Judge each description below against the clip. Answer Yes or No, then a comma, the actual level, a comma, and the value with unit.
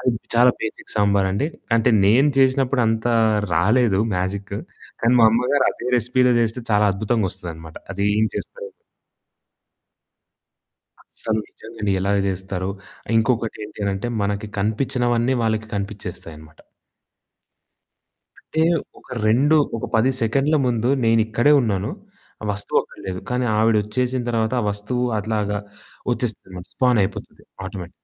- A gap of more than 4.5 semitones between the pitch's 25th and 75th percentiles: No, average, 3.6 semitones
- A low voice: Yes, low, 110 Hz